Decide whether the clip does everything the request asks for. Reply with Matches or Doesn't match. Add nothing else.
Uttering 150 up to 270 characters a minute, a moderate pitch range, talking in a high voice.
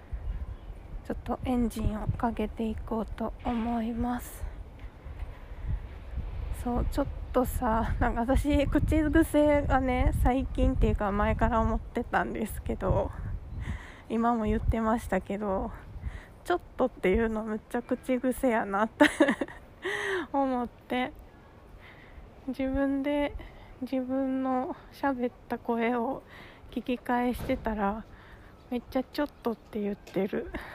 Matches